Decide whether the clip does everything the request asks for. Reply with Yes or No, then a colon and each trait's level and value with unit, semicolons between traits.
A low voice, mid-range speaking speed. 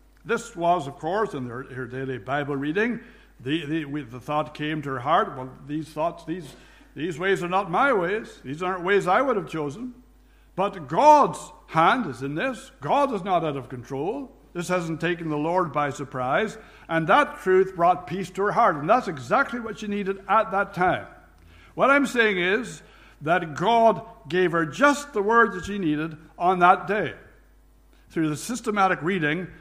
No: medium, 175 Hz; average, 185 wpm